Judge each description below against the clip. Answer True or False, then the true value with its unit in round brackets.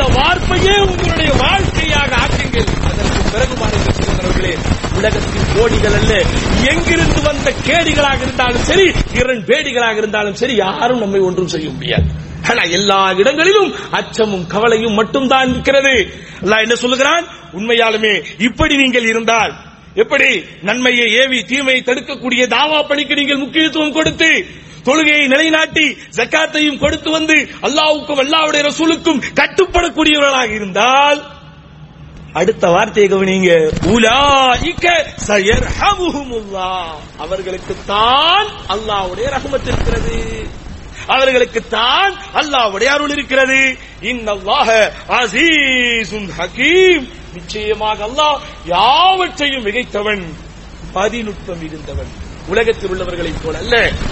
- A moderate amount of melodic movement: False (6.4 semitones)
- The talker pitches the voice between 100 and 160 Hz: False (250 Hz)